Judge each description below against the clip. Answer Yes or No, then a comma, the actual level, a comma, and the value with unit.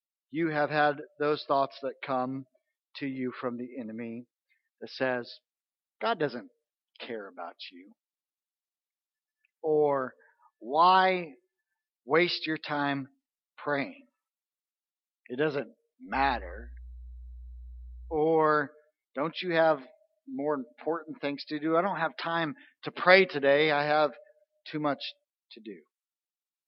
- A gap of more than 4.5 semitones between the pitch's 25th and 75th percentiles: Yes, average, 5.2 semitones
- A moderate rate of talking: No, slow, 110 wpm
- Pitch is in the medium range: Yes, medium, 150 Hz